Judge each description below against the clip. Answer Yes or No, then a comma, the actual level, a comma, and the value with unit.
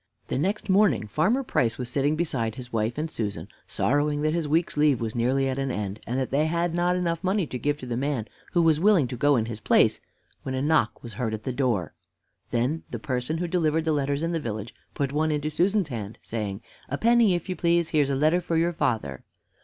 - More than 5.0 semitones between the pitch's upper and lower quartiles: Yes, wide, 5.6 semitones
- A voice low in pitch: No, medium, 145 Hz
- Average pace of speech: No, fast, 235 wpm